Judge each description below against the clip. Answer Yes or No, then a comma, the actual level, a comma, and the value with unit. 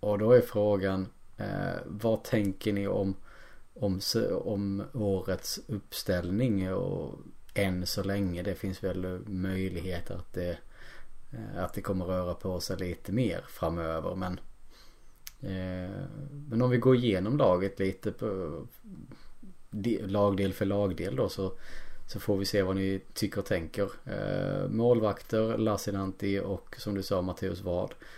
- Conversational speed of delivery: Yes, average, 140 wpm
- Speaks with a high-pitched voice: No, low, 100 Hz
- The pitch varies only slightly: Yes, narrow, 2.0 semitones